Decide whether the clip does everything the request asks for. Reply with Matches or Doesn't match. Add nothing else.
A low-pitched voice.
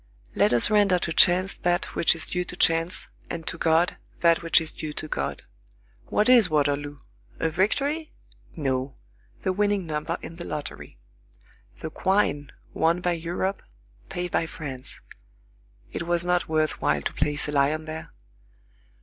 Doesn't match